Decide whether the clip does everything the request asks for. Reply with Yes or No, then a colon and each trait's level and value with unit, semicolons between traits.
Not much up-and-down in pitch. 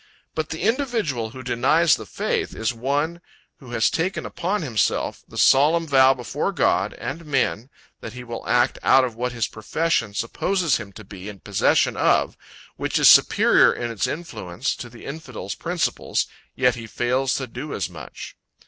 No: wide, 5.6 semitones